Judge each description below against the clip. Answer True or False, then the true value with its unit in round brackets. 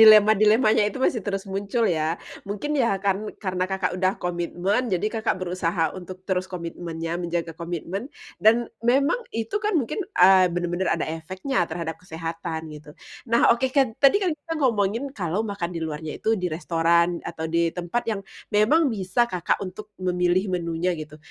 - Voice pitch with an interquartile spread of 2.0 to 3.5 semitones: False (4.1 semitones)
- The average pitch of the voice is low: False (185 Hz)